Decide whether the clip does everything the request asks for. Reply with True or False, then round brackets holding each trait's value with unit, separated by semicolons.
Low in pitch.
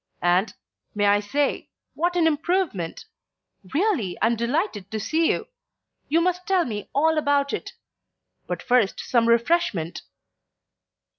False (280 Hz)